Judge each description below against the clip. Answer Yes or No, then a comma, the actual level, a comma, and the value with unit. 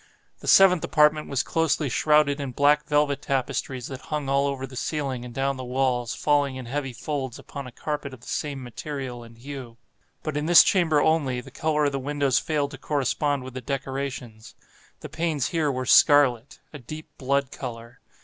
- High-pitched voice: No, medium, 140 Hz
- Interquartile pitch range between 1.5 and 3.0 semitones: Yes, narrow, 2.5 semitones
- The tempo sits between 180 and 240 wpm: Yes, average, 190 wpm